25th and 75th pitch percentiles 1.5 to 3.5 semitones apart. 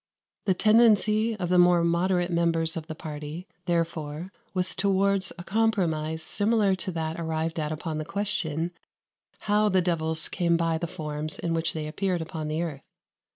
Yes: average, 3.0 semitones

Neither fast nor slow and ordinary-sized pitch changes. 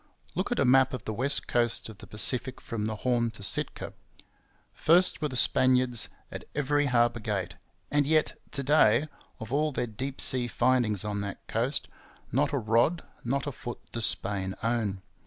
Yes: average, 180 wpm; average, 4.1 semitones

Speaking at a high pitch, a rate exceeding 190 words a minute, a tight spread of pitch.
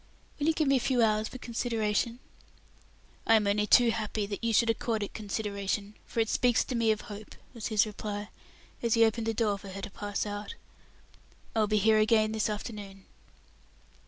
Yes: high, 215 Hz; average, 200 wpm; narrow, 1.8 semitones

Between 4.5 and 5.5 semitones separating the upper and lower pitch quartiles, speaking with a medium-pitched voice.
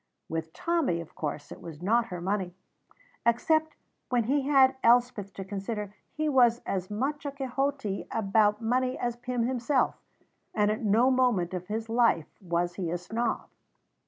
No: average, 4.9 semitones; high, 225 Hz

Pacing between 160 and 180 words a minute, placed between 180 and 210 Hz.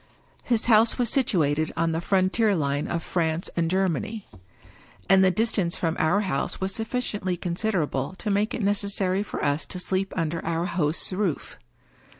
Yes: average, 165 wpm; medium, 185 Hz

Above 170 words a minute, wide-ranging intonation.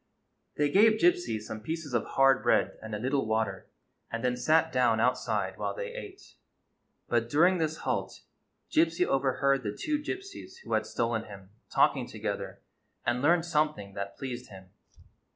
No: average, 160 wpm; wide, 6.7 semitones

